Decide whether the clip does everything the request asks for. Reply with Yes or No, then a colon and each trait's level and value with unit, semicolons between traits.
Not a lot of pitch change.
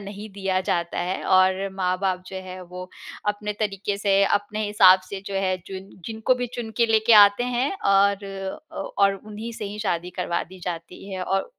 Yes: narrow, 2.1 semitones